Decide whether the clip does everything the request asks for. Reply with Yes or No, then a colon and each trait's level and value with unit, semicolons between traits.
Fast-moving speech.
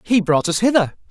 Yes: fast, 215 wpm